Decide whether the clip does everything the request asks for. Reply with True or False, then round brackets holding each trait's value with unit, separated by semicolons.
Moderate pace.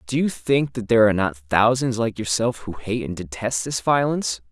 False (215 wpm)